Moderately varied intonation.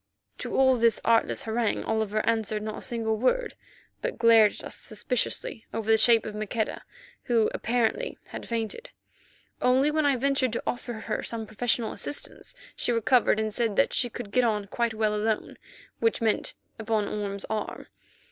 No: narrow, 2.0 semitones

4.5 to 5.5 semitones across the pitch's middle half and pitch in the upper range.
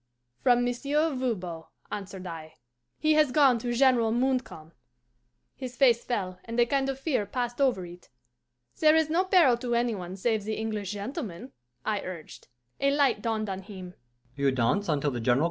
Yes: average, 5.2 semitones; high, 240 Hz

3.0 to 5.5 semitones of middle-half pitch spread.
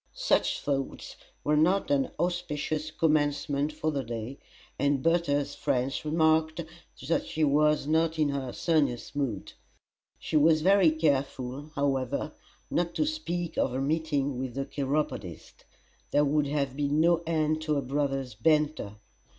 No: narrow, 2.5 semitones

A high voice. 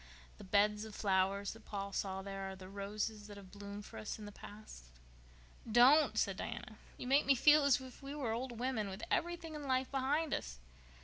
Yes: high, 215 Hz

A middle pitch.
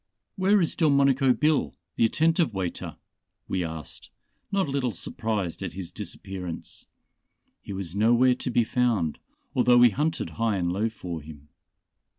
No: low, 115 Hz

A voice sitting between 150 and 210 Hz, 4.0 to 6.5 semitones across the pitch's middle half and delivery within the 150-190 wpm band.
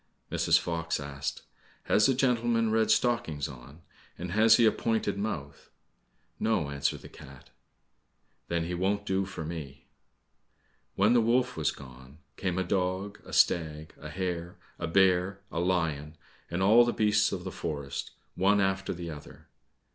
No: very low, 90 Hz; average, 4.9 semitones; average, 155 wpm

